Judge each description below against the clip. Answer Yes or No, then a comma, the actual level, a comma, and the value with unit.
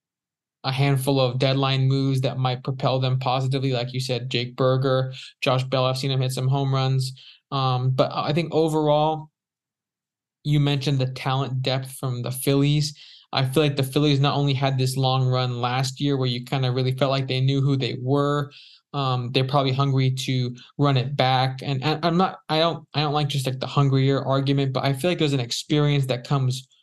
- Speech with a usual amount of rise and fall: No, narrow, 1.6 semitones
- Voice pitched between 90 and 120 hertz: No, low, 135 Hz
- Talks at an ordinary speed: No, fast, 210 wpm